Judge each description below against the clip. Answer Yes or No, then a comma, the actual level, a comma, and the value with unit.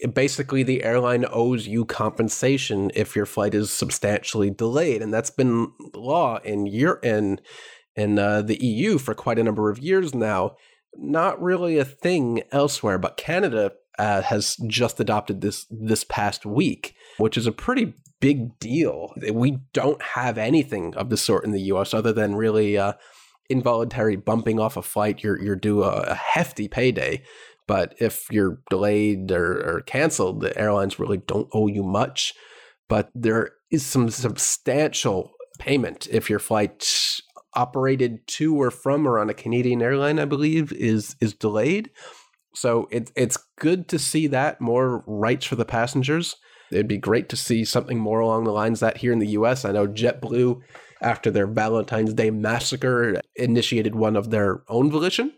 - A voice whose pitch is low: Yes, low, 115 Hz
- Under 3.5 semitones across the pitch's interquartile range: No, average, 3.8 semitones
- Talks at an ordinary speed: Yes, average, 165 wpm